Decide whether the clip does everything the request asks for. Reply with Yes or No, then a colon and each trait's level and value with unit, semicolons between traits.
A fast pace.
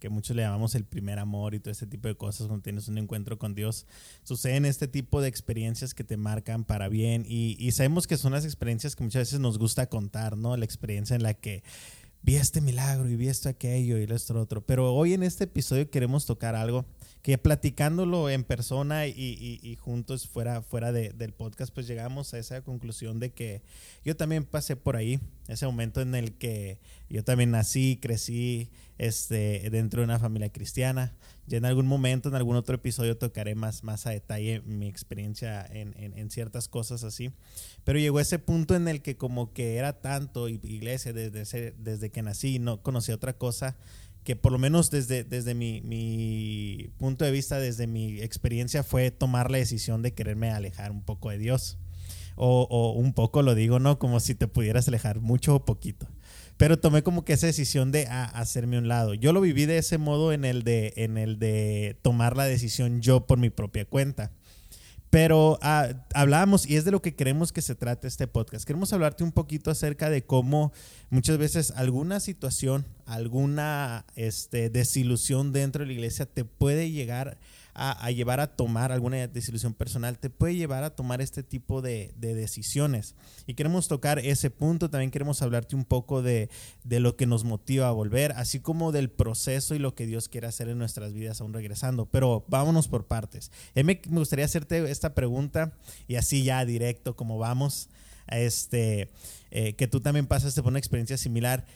Yes: fast, 195 wpm